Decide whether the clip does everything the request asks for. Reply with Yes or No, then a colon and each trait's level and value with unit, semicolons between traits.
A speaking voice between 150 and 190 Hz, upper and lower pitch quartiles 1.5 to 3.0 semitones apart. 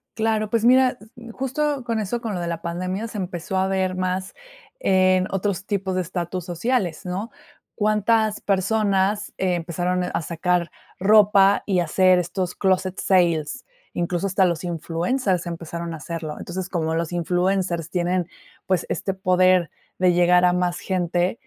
Yes: medium, 185 Hz; narrow, 2.4 semitones